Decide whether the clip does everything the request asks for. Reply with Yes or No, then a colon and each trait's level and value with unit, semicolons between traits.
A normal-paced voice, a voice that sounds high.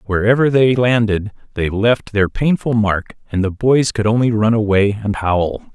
No: average, 180 wpm; low, 110 Hz